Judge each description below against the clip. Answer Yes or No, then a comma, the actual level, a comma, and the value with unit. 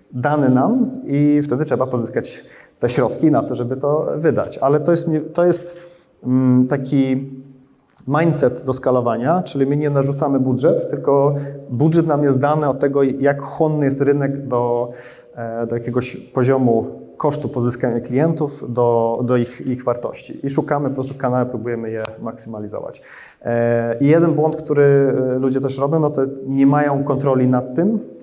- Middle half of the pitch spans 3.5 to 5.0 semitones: No, average, 2.9 semitones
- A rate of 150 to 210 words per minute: Yes, average, 155 wpm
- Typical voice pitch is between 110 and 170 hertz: Yes, low, 135 Hz